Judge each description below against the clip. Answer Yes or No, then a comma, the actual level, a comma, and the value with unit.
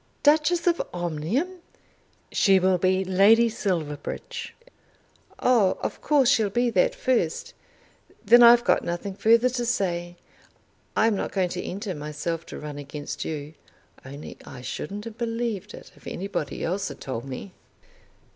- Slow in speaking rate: No, average, 145 wpm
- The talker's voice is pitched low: No, high, 195 Hz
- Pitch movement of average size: No, wide, 6.0 semitones